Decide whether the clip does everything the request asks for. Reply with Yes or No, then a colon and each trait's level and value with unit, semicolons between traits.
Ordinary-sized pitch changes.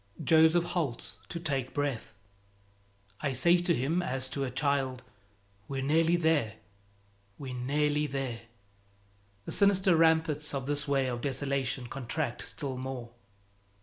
Yes: average, 3.6 semitones